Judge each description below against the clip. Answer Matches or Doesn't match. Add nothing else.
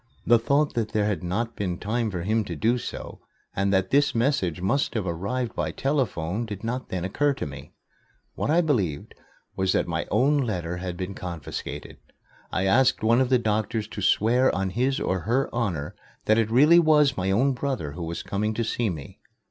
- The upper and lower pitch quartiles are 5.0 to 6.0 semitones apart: Matches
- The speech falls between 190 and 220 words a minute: Matches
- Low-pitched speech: Matches